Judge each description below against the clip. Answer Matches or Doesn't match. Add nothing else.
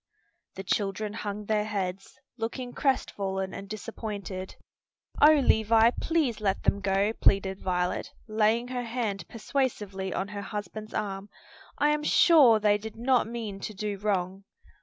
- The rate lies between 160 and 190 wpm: Doesn't match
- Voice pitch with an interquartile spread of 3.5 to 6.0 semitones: Doesn't match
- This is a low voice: Doesn't match